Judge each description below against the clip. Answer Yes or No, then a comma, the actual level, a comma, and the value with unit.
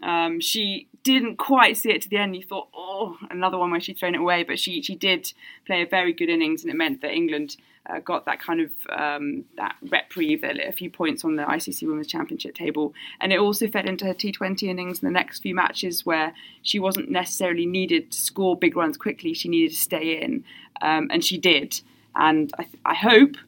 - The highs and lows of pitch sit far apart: Yes, wide, 8.2 semitones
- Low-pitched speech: No, high, 190 Hz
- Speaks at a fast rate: Yes, fast, 225 wpm